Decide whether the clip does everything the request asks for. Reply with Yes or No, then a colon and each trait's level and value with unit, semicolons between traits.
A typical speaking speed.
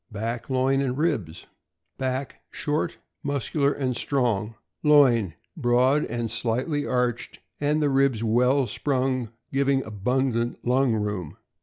No: slow, 125 wpm